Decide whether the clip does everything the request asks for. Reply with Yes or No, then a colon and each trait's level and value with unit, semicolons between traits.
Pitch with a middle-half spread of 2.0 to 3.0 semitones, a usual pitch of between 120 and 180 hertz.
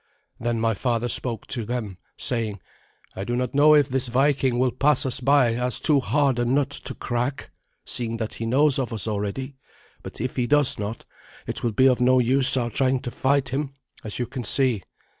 Yes: narrow, 2.6 semitones; low, 125 Hz